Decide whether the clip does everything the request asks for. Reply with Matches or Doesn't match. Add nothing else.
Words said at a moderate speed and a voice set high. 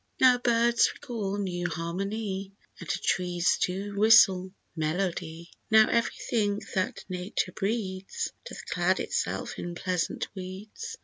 Doesn't match